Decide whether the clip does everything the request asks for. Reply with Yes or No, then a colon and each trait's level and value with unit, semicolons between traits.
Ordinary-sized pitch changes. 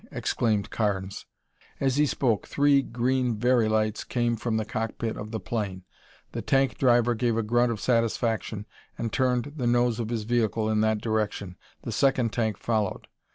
No: narrow, 2.1 semitones